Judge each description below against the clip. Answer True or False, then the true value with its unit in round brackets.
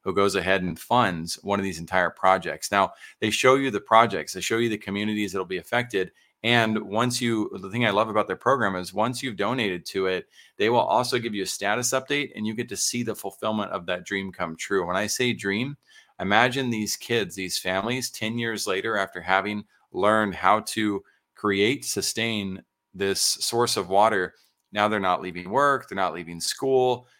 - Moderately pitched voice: False (105 Hz)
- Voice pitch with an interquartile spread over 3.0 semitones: True (3.7 semitones)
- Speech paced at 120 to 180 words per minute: False (205 wpm)